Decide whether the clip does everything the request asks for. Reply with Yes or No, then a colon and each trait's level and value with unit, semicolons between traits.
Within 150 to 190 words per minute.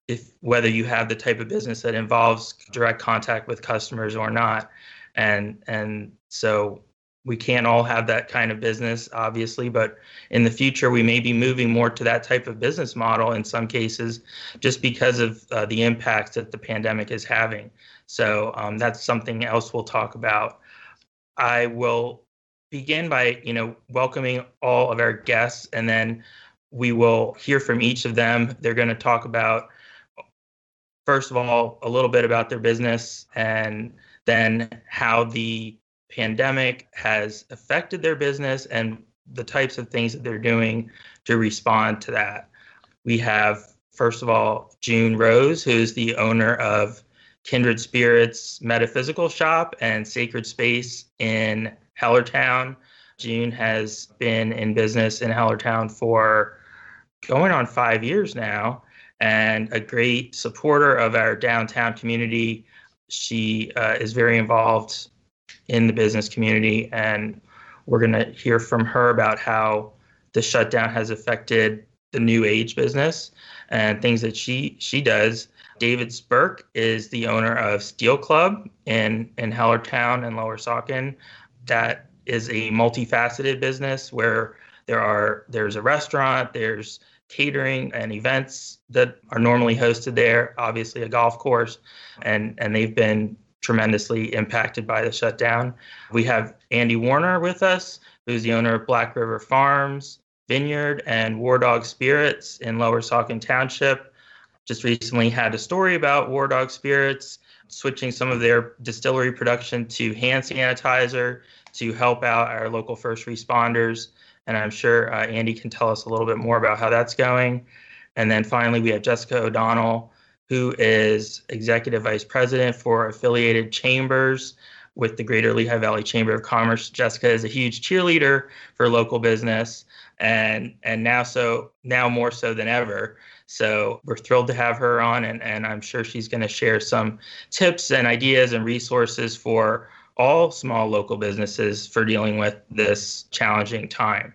Yes: average, 155 wpm